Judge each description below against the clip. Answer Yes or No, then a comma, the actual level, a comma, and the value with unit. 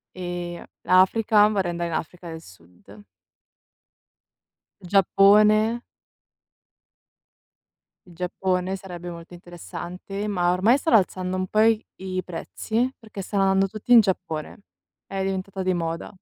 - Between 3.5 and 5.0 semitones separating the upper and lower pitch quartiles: No, average, 2.8 semitones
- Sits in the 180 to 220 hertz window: Yes, medium, 185 Hz